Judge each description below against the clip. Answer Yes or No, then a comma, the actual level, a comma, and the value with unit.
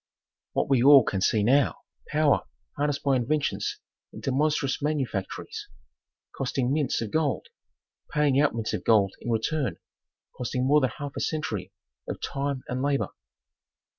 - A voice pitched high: No, medium, 140 Hz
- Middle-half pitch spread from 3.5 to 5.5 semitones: No, average, 3.1 semitones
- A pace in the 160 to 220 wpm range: No, average, 145 wpm